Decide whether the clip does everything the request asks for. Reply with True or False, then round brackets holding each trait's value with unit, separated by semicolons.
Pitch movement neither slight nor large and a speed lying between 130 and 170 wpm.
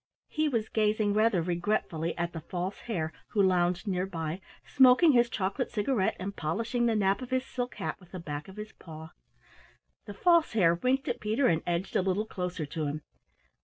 False (5.0 semitones; 195 wpm)